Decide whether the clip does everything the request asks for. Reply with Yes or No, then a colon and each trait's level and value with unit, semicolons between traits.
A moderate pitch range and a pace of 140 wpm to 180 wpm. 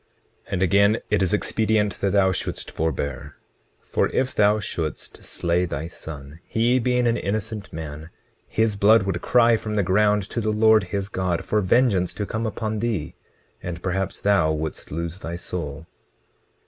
Yes: average, 4.2 semitones; average, 170 wpm